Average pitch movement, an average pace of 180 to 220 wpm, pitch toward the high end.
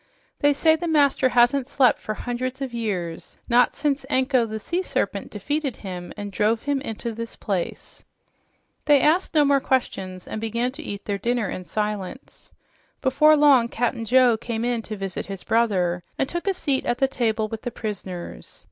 Yes: average, 4.5 semitones; average, 185 wpm; high, 240 Hz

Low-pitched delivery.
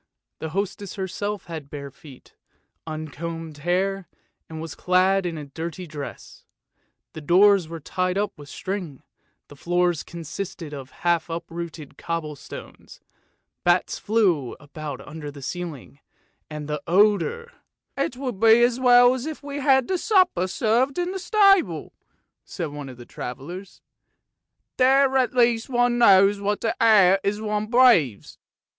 No: medium, 185 Hz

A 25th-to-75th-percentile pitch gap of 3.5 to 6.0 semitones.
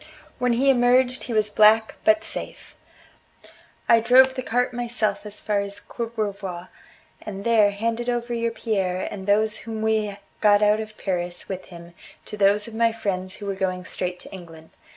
No: average, 2.9 semitones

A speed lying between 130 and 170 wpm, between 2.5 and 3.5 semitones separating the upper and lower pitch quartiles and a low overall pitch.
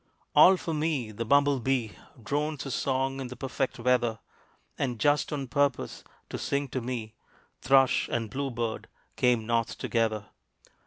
Yes: average, 155 wpm; average, 3.2 semitones; low, 130 Hz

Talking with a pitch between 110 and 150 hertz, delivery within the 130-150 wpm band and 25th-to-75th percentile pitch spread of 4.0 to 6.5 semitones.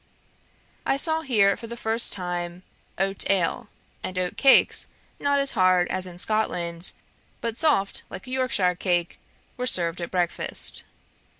No: high, 195 Hz; average, 140 wpm; average, 4.9 semitones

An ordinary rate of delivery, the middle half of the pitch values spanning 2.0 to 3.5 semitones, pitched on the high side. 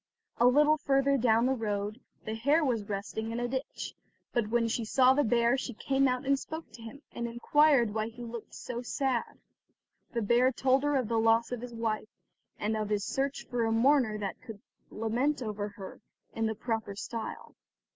Yes: average, 195 wpm; average, 3.2 semitones; high, 235 Hz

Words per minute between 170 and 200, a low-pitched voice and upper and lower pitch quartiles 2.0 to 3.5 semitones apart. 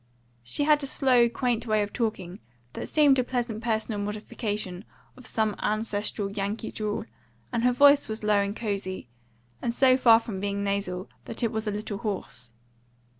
No: average, 175 wpm; high, 215 Hz; average, 2.9 semitones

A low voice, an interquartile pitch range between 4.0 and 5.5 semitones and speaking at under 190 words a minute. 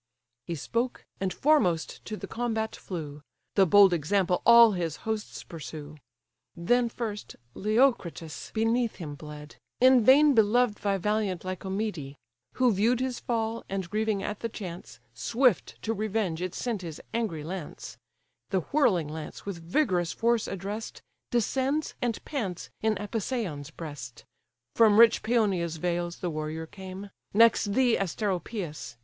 No: high, 200 Hz; average, 5.2 semitones; average, 140 wpm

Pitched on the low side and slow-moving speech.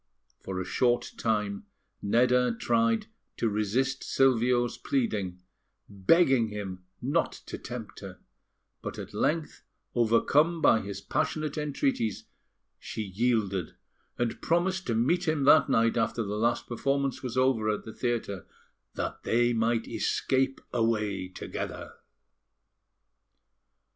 Yes: low, 115 Hz; slow, 120 wpm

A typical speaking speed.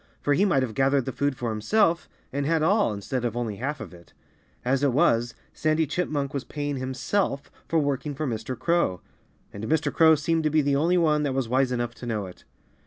No: fast, 220 wpm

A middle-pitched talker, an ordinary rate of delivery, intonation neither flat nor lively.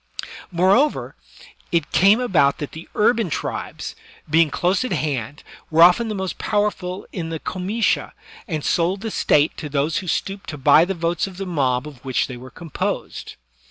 Yes: medium, 170 Hz; average, 175 wpm; average, 4.6 semitones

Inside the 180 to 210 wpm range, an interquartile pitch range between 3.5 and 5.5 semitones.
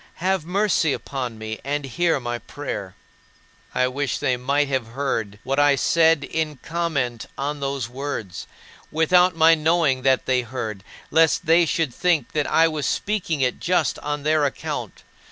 No: average, 160 wpm; average, 4.2 semitones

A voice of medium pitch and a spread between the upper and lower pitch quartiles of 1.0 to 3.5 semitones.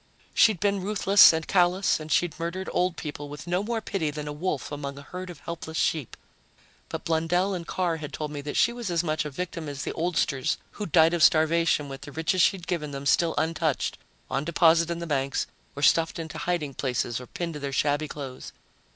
Yes: medium, 160 Hz; average, 3.2 semitones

